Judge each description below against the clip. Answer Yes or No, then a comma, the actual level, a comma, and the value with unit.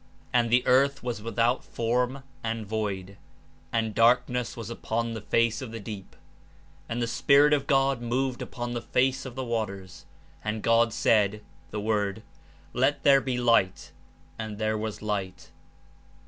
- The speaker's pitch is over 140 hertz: No, low, 115 Hz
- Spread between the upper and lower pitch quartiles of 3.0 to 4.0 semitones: No, narrow, 2.6 semitones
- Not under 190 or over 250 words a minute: No, average, 165 wpm